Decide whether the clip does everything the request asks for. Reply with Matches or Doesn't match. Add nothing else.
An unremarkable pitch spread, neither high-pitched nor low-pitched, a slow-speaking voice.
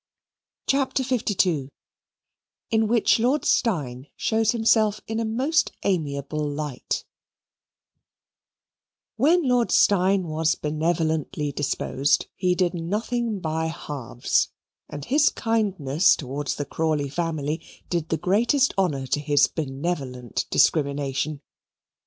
Doesn't match